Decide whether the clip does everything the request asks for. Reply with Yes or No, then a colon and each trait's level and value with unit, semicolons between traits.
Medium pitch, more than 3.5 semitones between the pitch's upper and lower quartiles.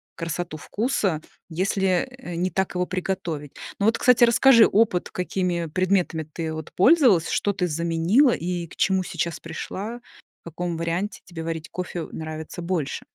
No: medium, 180 Hz; average, 3.0 semitones